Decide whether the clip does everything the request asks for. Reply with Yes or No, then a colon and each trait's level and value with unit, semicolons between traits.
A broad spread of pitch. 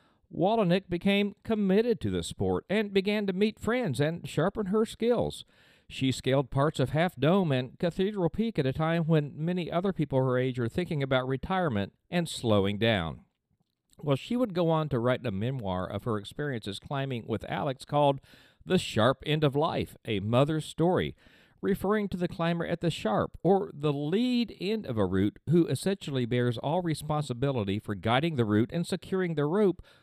Yes: wide, 6.6 semitones